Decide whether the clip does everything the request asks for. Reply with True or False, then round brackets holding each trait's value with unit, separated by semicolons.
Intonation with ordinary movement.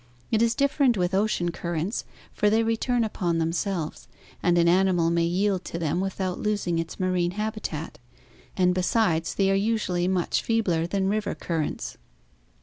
True (3.6 semitones)